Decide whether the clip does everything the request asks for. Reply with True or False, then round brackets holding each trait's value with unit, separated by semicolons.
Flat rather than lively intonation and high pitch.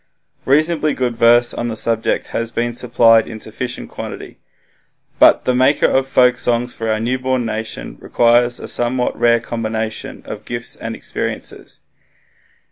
False (1.6 semitones; 120 Hz)